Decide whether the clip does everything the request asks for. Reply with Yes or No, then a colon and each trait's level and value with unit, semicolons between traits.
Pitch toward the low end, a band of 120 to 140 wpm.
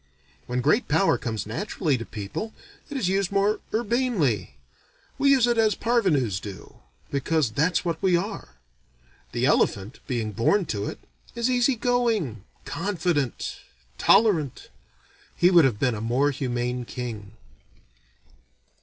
No: medium, 160 Hz; slow, 135 wpm